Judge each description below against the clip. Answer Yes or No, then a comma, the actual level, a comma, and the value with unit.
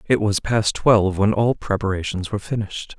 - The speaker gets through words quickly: No, average, 180 wpm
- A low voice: Yes, low, 105 Hz